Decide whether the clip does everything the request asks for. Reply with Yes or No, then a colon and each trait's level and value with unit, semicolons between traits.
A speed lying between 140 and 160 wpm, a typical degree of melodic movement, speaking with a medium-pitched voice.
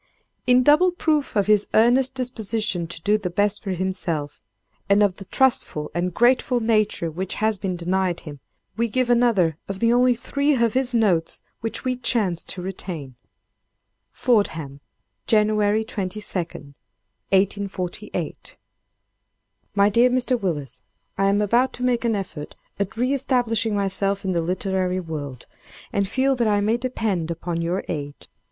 No: average, 150 wpm; average, 4.9 semitones; high, 205 Hz